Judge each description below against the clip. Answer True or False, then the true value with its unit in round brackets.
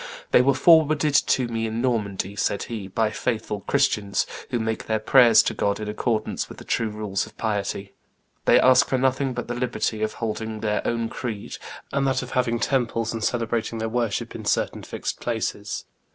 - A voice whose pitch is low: True (115 Hz)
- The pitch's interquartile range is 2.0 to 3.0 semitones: True (2.7 semitones)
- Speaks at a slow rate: False (190 wpm)